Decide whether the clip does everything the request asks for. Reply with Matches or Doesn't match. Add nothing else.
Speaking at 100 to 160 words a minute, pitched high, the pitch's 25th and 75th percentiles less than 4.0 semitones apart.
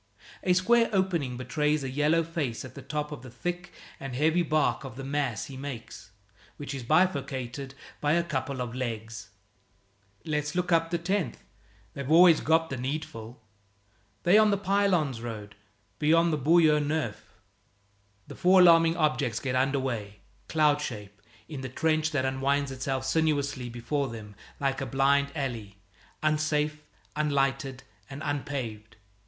Doesn't match